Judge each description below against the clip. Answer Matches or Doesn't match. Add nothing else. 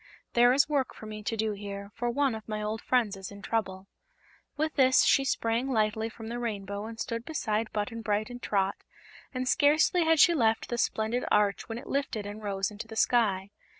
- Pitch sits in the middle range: Doesn't match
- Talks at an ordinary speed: Doesn't match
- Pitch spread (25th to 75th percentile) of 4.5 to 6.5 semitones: Doesn't match